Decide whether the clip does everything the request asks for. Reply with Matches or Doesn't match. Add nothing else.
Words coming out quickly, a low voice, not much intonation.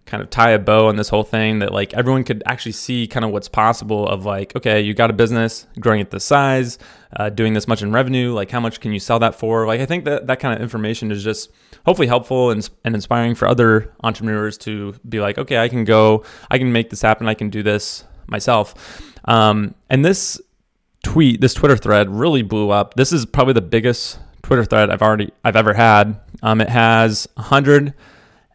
Matches